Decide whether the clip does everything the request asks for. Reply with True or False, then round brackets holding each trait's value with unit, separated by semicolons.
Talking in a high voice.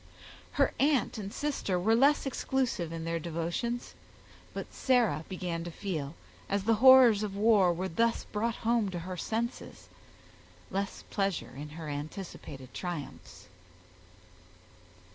True (195 Hz)